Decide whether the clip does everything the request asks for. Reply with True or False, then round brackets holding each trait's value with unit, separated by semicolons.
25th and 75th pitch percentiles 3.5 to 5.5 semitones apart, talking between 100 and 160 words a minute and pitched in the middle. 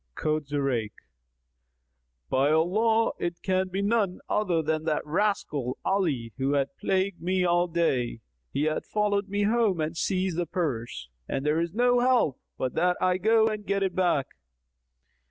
True (5.0 semitones; 155 wpm; 175 Hz)